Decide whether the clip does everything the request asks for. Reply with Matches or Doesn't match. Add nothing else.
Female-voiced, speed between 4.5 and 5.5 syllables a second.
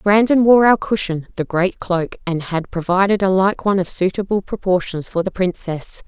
Matches